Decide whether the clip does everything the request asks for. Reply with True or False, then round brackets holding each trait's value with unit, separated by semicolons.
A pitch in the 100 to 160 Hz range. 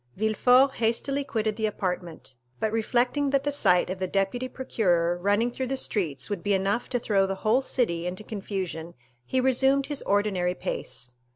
False (215 Hz)